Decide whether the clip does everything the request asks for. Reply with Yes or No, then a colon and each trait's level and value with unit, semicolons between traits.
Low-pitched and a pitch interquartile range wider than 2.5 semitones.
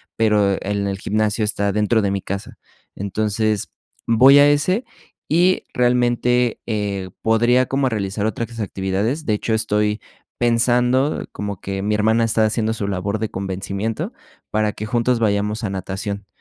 Yes: low, 110 Hz; average, 2.9 semitones